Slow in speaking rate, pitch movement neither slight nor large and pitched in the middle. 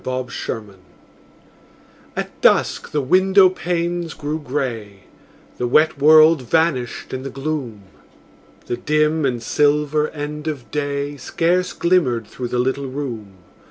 Yes: slow, 125 wpm; average, 3.9 semitones; medium, 145 Hz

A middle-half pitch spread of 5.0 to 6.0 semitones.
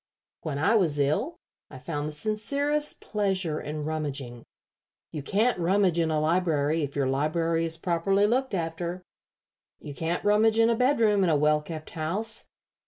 Yes: wide, 5.4 semitones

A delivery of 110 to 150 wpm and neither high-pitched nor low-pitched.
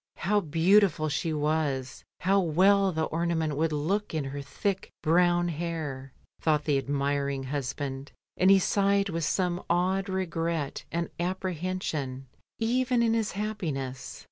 Yes: slow, 135 wpm; medium, 165 Hz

